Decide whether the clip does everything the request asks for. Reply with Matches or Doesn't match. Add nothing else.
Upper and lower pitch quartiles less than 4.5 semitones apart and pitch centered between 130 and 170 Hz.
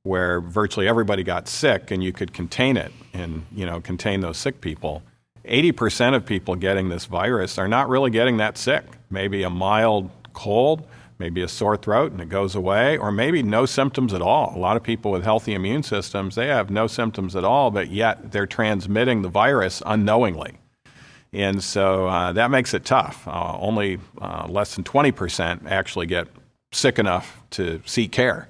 Doesn't match